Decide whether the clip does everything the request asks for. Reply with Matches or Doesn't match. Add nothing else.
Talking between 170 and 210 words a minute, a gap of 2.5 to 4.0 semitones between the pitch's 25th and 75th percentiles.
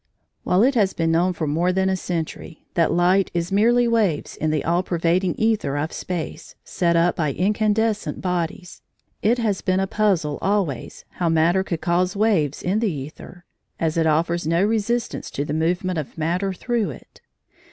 Matches